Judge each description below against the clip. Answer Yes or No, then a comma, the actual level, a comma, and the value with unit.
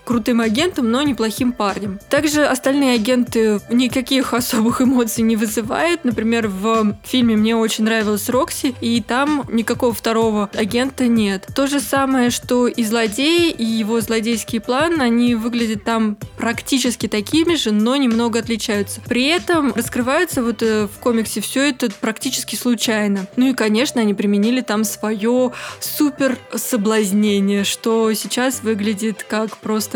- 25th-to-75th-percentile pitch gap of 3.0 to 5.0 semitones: No, narrow, 2.6 semitones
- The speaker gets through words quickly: No, average, 140 wpm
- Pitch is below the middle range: No, high, 235 Hz